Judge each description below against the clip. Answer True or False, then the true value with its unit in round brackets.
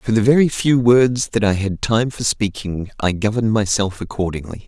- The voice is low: True (110 Hz)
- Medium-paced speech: True (195 wpm)